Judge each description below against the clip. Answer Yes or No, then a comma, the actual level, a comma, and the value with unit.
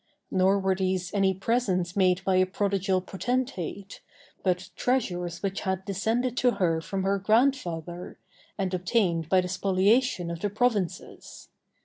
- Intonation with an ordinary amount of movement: No, narrow, 2.2 semitones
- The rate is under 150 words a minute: Yes, average, 140 wpm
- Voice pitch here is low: No, high, 190 Hz